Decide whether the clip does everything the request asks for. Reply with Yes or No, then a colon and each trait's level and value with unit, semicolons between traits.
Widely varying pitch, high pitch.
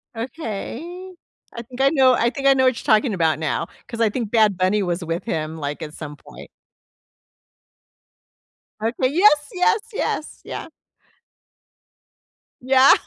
Yes: wide, 7.0 semitones; high, 230 Hz